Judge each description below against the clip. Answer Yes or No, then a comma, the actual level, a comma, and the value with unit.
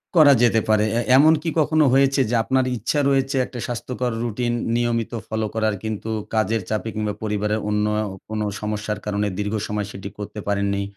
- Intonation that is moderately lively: Yes, average, 3.0 semitones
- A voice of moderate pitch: No, low, 110 Hz